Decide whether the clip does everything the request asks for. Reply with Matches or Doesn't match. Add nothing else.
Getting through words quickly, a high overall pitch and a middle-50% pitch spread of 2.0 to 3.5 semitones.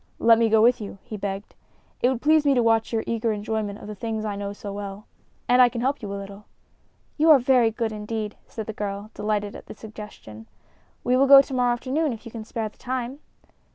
Matches